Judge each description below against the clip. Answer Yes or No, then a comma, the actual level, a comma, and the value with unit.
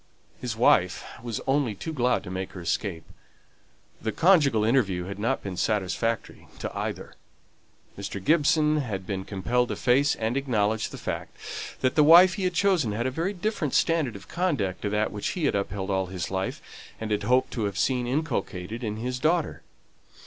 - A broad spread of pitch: Yes, wide, 6.6 semitones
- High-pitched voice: No, low, 115 Hz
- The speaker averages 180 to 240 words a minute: Yes, average, 185 wpm